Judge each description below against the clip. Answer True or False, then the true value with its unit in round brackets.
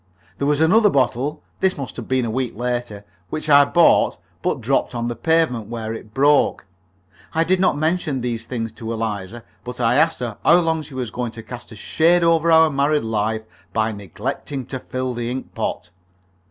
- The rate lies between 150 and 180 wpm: False (200 wpm)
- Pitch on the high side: False (125 Hz)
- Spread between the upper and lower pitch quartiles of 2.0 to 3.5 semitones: False (5.2 semitones)